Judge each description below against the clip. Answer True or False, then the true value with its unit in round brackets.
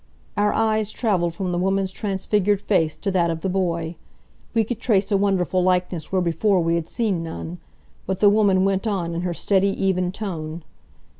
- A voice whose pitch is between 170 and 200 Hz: True (190 Hz)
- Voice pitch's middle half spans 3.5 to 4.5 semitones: False (2.9 semitones)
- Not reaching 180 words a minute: False (190 wpm)